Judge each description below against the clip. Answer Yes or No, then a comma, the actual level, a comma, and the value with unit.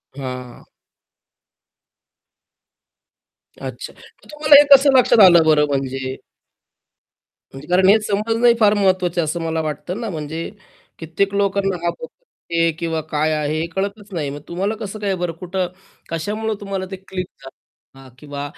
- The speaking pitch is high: No, medium, 175 Hz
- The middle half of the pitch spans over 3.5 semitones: Yes, average, 4.7 semitones